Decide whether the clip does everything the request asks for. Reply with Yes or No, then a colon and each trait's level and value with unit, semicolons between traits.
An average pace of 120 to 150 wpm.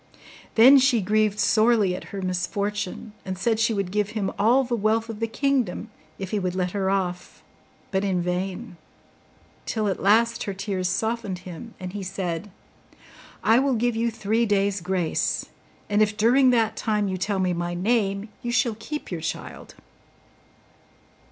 No: average, 170 wpm